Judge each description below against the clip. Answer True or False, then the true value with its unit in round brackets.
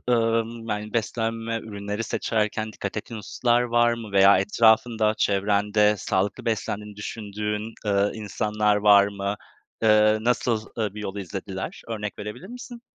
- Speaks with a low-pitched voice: True (105 Hz)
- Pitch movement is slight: True (1.8 semitones)